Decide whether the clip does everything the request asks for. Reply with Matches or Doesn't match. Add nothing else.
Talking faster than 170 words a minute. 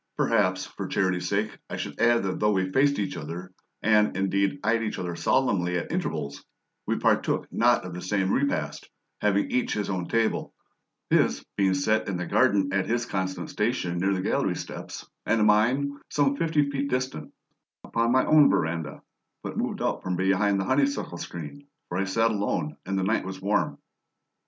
Matches